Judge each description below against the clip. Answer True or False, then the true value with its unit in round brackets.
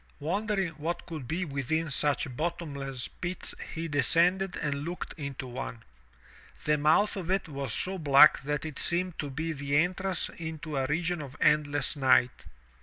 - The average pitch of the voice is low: False (155 Hz)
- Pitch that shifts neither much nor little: True (3.6 semitones)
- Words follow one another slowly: False (165 wpm)